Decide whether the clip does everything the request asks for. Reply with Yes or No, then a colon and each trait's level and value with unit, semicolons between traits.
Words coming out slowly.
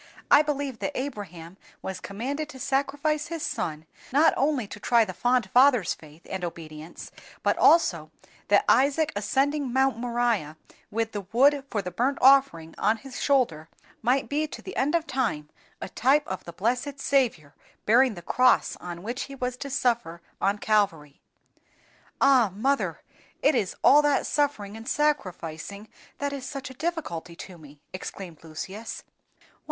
No: average, 160 wpm